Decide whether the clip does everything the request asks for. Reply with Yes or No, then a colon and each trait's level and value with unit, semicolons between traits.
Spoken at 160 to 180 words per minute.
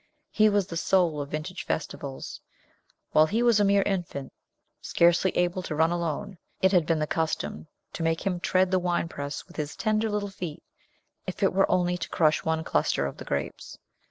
No: average, 190 wpm